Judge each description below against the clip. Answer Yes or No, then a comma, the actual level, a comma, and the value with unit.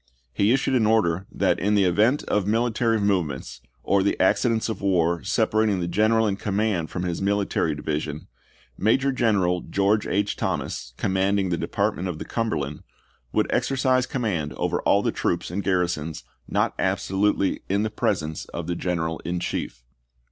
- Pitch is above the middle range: No, very low, 95 Hz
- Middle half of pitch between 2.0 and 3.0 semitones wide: No, average, 4.1 semitones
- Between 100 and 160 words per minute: No, average, 170 wpm